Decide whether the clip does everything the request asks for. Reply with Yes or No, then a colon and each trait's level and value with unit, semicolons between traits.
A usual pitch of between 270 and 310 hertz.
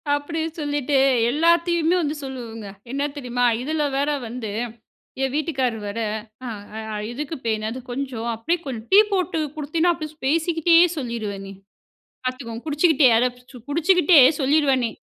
Yes: very high, 285 Hz